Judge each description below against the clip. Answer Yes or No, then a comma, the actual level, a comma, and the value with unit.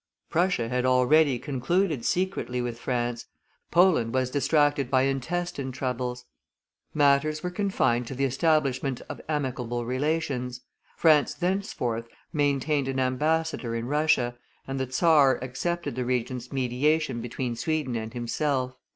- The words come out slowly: Yes, slow, 125 wpm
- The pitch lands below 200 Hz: Yes, low, 135 Hz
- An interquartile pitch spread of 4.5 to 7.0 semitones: No, average, 3.7 semitones